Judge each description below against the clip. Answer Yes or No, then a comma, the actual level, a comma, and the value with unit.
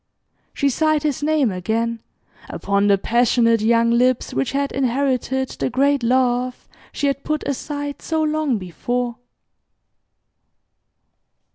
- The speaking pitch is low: No, very high, 255 Hz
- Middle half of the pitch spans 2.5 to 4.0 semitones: Yes, average, 3.4 semitones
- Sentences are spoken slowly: Yes, slow, 120 wpm